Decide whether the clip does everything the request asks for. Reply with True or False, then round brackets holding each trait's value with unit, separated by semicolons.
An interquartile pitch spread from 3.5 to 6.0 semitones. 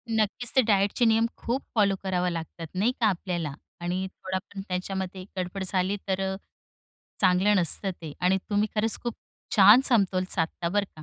False (2.5 semitones)